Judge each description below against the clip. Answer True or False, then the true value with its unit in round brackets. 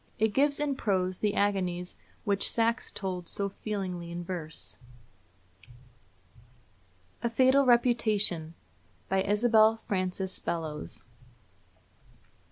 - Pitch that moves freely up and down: False (4.0 semitones)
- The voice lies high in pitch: True (200 Hz)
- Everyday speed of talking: False (95 wpm)